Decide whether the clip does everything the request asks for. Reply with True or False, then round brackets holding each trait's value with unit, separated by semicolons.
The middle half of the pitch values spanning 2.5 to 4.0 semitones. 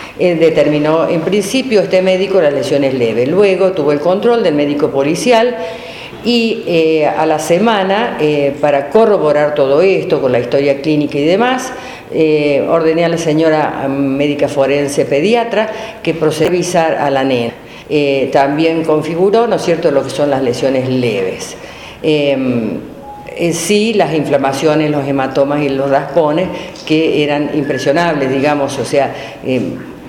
False (4.5 semitones)